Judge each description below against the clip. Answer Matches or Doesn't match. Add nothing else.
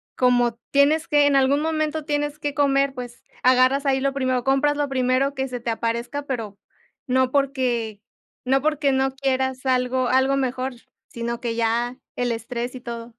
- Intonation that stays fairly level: Matches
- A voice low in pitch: Doesn't match